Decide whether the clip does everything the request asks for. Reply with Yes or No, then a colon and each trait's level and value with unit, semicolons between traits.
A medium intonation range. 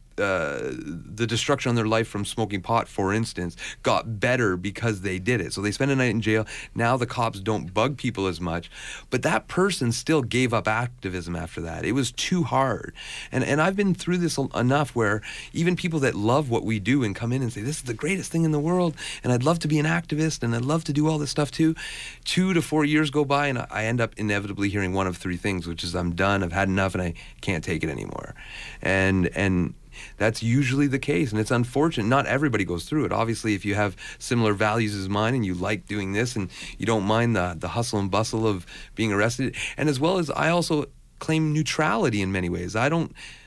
No: wide, 6.0 semitones